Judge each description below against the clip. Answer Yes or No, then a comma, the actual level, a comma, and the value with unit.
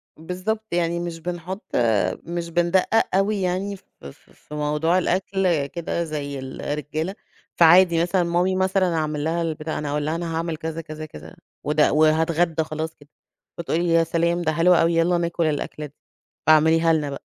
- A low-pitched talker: No, medium, 165 Hz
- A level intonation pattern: Yes, narrow, 2.2 semitones